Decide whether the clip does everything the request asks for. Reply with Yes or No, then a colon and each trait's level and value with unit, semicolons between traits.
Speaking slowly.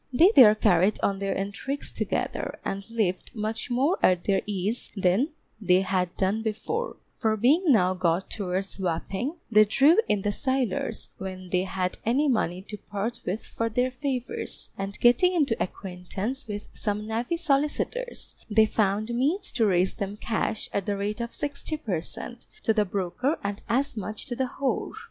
No: average, 170 wpm